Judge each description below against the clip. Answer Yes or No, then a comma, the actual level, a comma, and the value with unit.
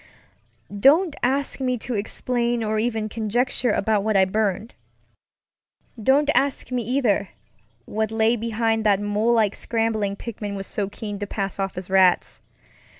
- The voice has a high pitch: Yes, high, 220 Hz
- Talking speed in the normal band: Yes, average, 150 wpm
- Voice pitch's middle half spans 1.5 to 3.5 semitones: Yes, average, 2.9 semitones